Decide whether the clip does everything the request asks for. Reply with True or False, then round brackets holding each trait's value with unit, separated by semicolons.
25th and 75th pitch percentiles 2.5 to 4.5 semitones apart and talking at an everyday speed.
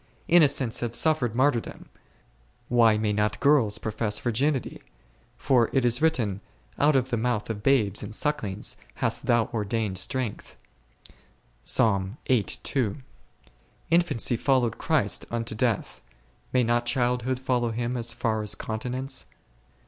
False (3.0 semitones; 125 wpm)